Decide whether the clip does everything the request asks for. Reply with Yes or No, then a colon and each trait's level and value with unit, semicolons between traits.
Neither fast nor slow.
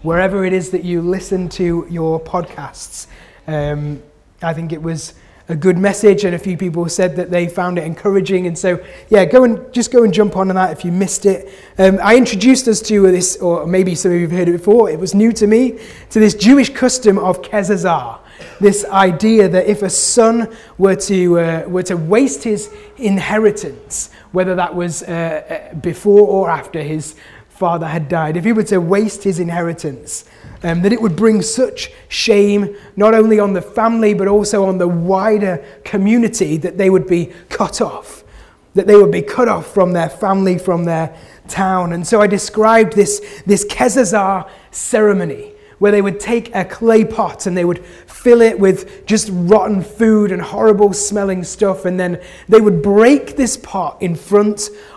Yes: average, 190 wpm